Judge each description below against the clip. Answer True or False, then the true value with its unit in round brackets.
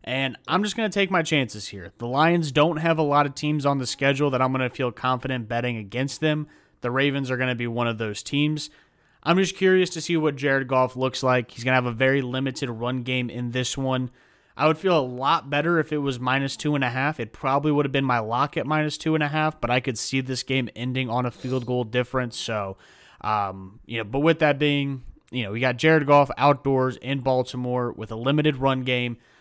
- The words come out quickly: True (250 wpm)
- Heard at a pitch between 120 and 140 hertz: True (130 Hz)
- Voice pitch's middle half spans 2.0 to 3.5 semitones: True (3.0 semitones)